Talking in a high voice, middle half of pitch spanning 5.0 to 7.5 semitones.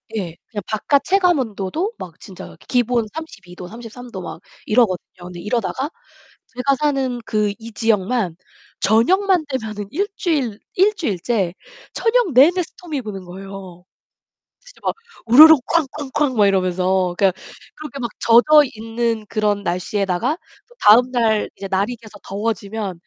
Yes: high, 225 Hz; wide, 6.0 semitones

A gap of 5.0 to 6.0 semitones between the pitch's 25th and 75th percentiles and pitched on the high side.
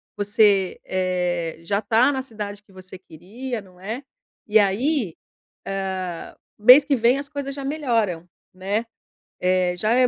Yes: wide, 5.4 semitones; high, 210 Hz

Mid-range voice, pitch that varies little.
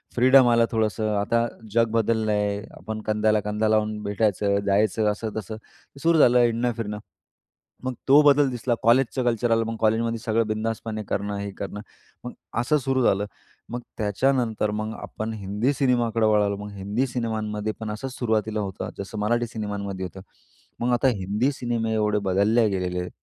No: low, 110 Hz; narrow, 2.3 semitones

